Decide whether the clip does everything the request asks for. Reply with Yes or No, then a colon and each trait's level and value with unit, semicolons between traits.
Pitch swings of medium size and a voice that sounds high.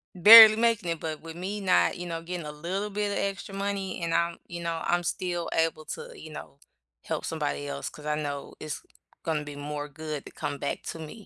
No: average, 4.0 semitones; medium, 170 Hz